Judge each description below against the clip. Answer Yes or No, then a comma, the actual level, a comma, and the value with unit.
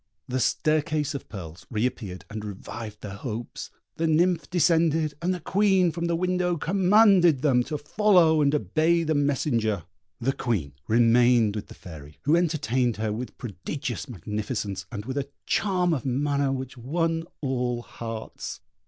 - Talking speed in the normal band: Yes, average, 155 wpm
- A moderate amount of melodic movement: No, wide, 6.5 semitones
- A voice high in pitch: No, low, 135 Hz